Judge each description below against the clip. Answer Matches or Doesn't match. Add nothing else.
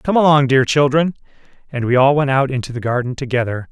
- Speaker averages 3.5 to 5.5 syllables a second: Doesn't match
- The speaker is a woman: Doesn't match